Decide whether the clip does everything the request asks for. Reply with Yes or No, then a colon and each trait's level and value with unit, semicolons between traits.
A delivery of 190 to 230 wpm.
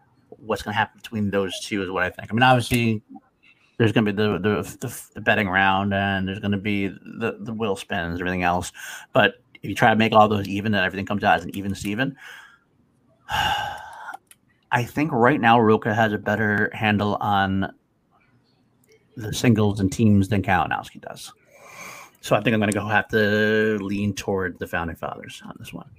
Yes: average, 200 wpm